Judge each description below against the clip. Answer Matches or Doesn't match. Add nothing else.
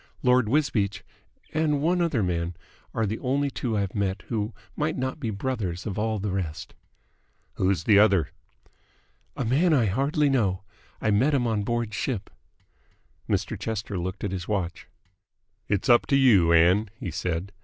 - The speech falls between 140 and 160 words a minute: Doesn't match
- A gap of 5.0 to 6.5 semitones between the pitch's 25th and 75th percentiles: Matches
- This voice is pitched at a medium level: Doesn't match